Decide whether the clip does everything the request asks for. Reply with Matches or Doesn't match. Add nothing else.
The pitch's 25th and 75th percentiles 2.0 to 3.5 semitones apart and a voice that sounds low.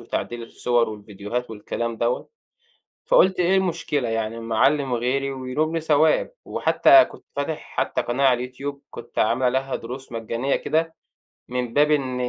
Doesn't match